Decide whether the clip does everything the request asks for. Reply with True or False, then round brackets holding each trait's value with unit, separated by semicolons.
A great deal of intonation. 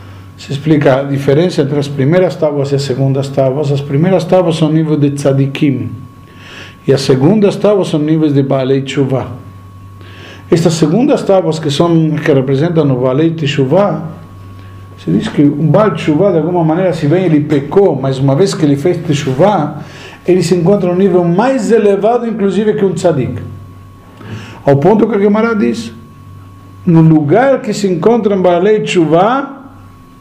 True (5.7 semitones)